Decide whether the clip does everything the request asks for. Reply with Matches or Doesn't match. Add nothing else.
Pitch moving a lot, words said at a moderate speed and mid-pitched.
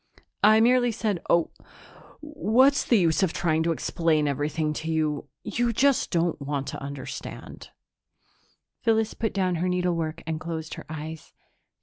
Matches